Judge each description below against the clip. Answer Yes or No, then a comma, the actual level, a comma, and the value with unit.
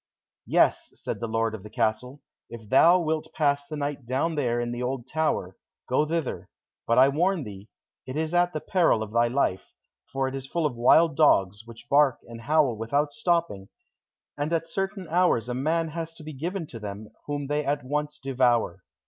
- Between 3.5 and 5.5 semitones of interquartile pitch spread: Yes, average, 5.2 semitones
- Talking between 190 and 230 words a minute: Yes, average, 200 wpm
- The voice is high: No, medium, 140 Hz